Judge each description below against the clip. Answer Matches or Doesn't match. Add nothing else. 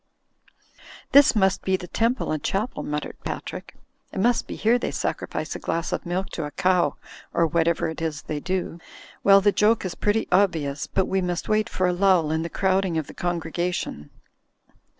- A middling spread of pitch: Matches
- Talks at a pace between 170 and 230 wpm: Matches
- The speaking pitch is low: Doesn't match